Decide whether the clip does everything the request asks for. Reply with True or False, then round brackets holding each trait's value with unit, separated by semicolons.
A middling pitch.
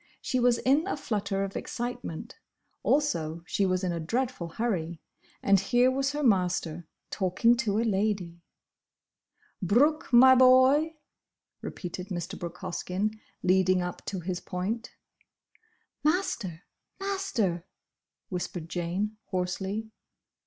False (200 Hz)